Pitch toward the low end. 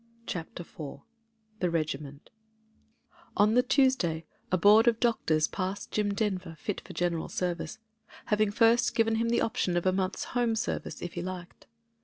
No: high, 190 Hz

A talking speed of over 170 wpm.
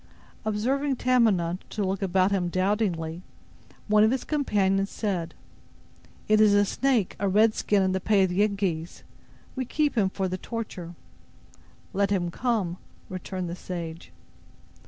No: average, 145 wpm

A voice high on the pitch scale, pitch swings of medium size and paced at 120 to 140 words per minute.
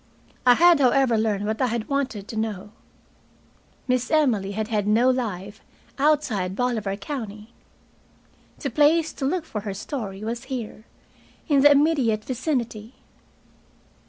Yes: high, 235 Hz; average, 4.6 semitones; slow, 135 wpm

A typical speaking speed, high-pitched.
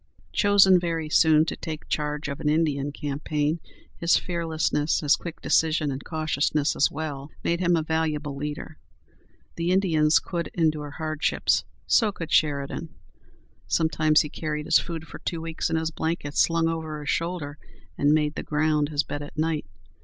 No: average, 165 wpm; medium, 155 Hz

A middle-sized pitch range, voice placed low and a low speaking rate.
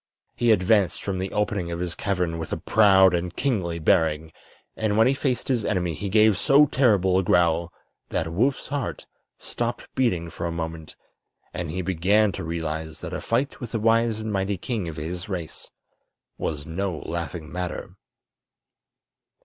No: average, 4.6 semitones; very low, 90 Hz; average, 170 wpm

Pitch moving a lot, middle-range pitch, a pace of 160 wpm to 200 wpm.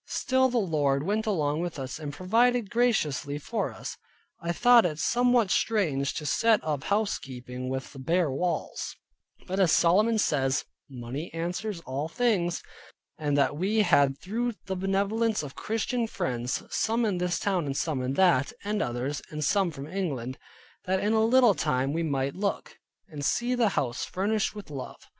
Yes: wide, 7.1 semitones; medium, 175 Hz; average, 170 wpm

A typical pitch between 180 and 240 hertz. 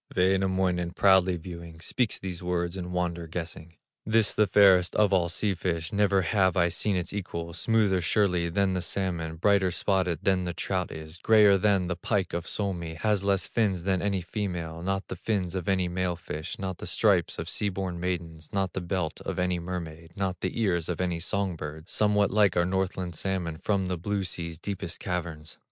No: very low, 90 Hz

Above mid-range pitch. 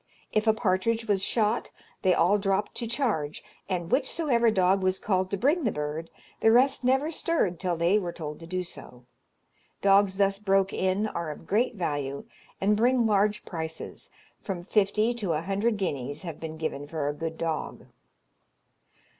Yes: high, 195 Hz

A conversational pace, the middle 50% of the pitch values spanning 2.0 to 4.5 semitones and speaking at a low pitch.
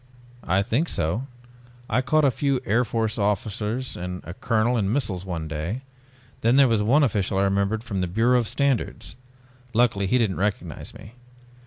Yes: average, 175 wpm; average, 4.2 semitones; low, 110 Hz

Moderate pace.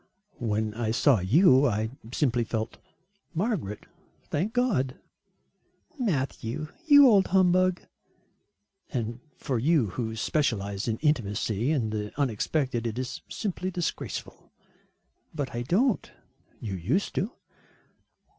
No: slow, 110 wpm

